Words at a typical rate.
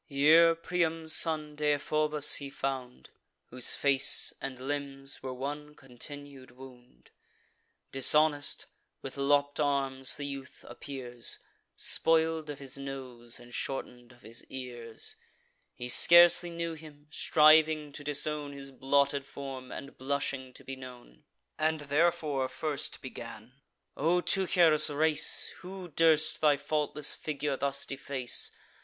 No: slow, 125 wpm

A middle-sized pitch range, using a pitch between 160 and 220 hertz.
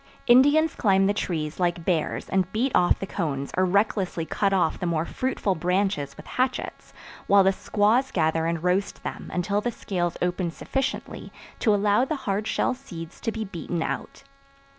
Yes: average, 3.9 semitones; high, 190 Hz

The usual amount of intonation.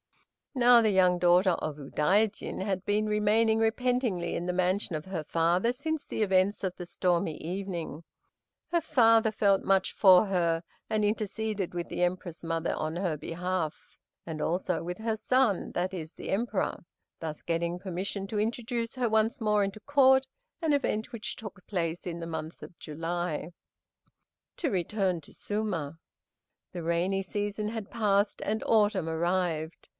Yes: average, 4.0 semitones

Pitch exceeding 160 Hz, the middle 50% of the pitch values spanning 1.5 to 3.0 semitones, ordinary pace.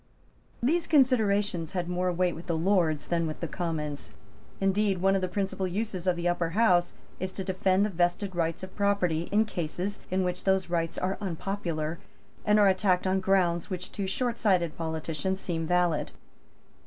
Yes: medium, 185 Hz; narrow, 2.4 semitones; average, 175 wpm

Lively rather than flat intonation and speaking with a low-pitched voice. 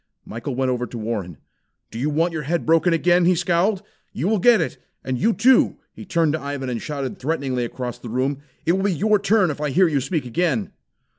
No: wide, 5.7 semitones; medium, 150 Hz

